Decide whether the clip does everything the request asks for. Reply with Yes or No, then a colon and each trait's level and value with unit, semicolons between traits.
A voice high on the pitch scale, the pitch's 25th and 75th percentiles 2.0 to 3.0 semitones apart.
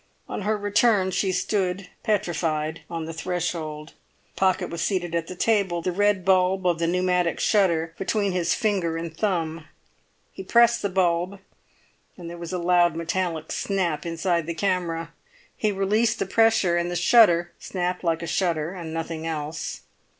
No: medium, 175 Hz; narrow, 2.6 semitones